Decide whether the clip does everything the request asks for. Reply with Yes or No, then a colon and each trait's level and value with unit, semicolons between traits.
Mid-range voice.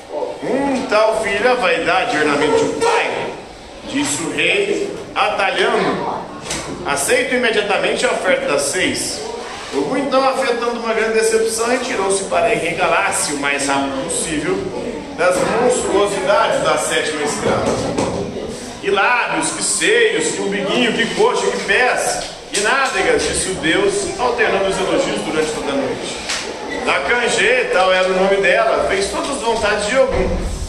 No: high, 245 Hz